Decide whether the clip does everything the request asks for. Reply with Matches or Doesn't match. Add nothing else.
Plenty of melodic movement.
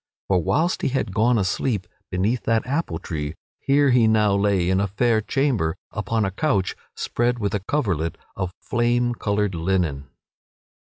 Doesn't match